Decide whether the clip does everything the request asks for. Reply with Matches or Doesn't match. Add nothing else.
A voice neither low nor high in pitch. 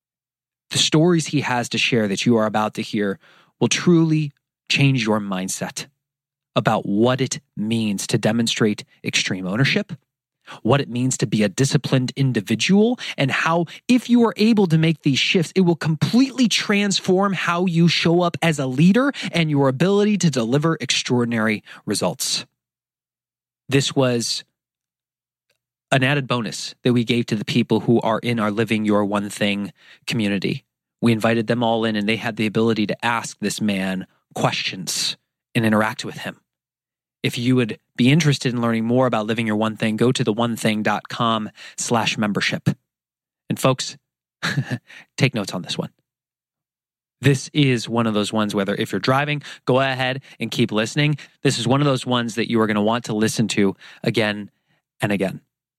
Doesn't match